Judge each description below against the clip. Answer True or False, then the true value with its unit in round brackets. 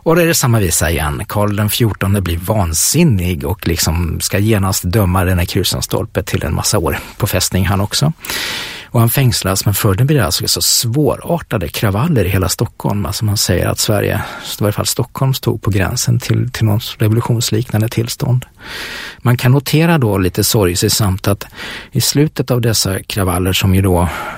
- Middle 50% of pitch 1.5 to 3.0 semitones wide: False (4.1 semitones)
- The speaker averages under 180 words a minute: False (190 wpm)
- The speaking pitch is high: False (110 Hz)